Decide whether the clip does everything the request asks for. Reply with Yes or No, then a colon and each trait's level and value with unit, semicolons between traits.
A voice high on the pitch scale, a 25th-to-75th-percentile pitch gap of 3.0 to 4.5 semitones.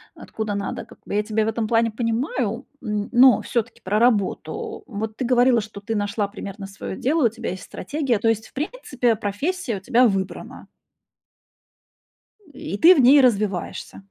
Yes: high, 225 Hz; average, 3.4 semitones